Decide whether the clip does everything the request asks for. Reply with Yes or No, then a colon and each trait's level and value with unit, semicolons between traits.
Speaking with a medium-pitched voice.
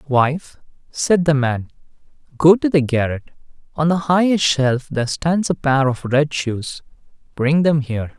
Yes: medium, 145 Hz